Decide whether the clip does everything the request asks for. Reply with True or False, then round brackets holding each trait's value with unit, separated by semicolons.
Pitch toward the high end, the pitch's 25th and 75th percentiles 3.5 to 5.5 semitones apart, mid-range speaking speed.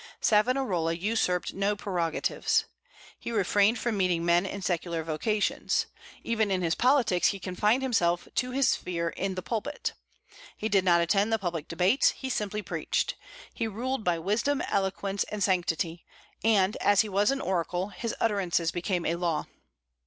True (195 Hz; 3.9 semitones; 160 wpm)